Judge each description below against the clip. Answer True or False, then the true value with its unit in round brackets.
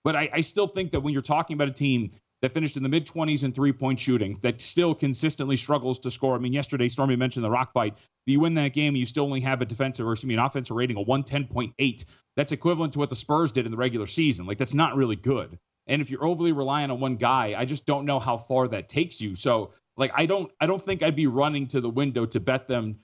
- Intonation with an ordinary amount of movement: True (3.0 semitones)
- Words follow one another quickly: True (265 wpm)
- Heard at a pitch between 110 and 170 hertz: True (135 Hz)